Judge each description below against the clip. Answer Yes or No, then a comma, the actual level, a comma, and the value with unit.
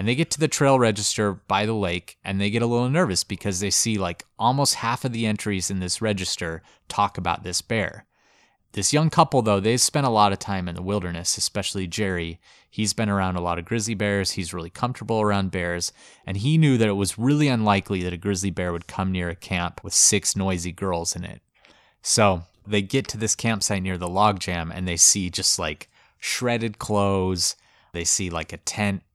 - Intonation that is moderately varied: Yes, average, 3.5 semitones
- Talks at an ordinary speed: No, fast, 215 wpm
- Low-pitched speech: Yes, low, 100 Hz